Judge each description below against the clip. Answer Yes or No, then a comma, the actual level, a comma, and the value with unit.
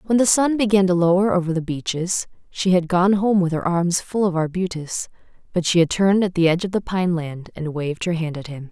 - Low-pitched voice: No, medium, 180 Hz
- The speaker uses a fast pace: Yes, fast, 240 wpm